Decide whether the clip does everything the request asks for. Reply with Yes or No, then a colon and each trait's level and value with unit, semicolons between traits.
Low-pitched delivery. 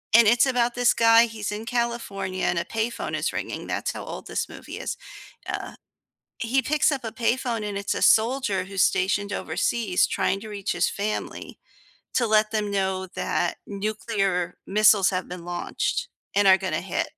No: high, 210 Hz